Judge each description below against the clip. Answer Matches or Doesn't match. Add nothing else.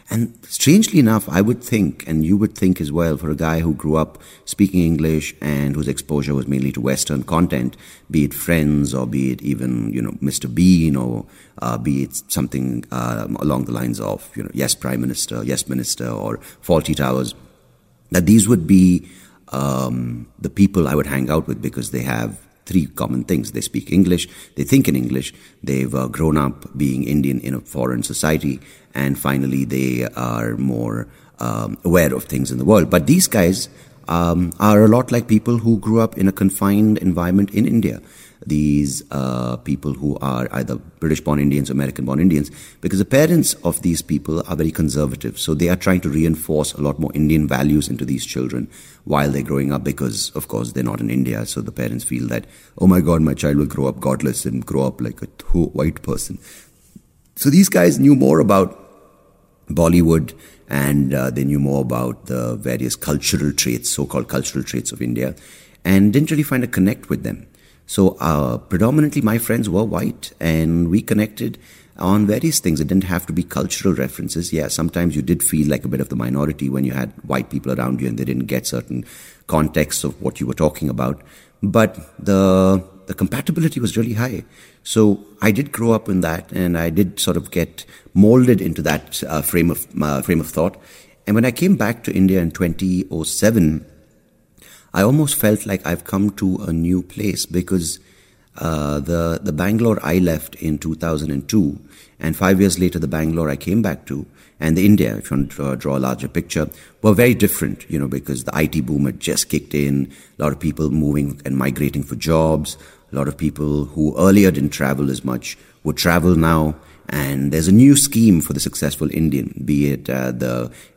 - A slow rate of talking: Doesn't match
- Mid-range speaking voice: Doesn't match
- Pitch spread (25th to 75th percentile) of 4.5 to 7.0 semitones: Matches